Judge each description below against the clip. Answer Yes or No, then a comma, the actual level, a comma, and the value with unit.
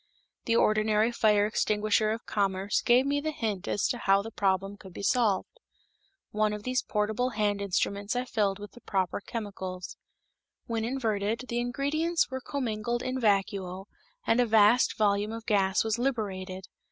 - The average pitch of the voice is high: Yes, high, 215 Hz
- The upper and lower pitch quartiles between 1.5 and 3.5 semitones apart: Yes, average, 3.1 semitones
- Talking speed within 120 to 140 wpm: No, average, 165 wpm